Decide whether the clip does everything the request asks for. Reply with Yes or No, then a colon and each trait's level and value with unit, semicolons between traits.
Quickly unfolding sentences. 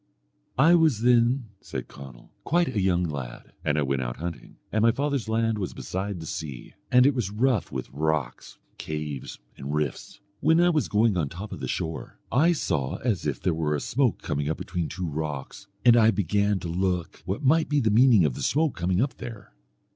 Yes: fast, 210 wpm